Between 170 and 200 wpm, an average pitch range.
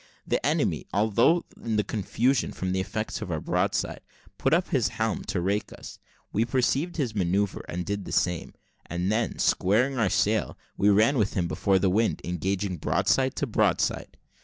Yes: average, 175 wpm; average, 3.9 semitones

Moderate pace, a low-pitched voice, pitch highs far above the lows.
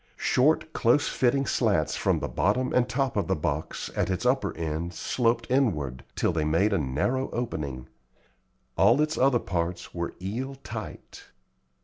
Yes: average, 155 wpm; low, 110 Hz; wide, 7.3 semitones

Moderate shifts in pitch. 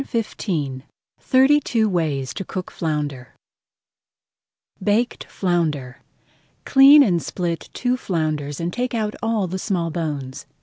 No: wide, 6.9 semitones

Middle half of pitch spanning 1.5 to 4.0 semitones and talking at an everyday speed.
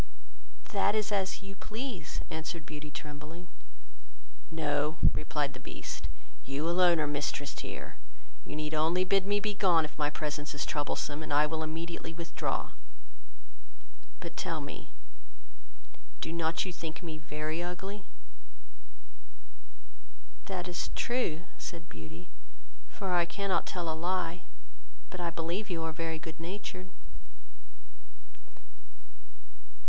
No: average, 3.1 semitones; slow, 125 wpm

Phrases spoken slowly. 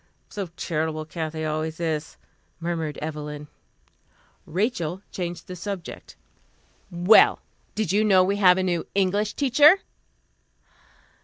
Yes: slow, 110 wpm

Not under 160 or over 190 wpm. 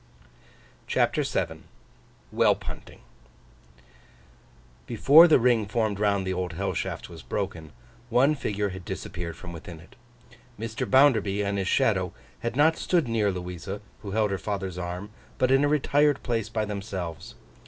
No: average, 150 wpm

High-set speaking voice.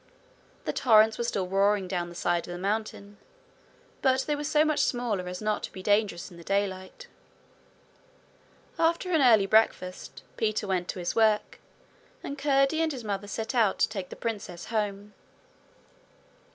Yes: high, 210 Hz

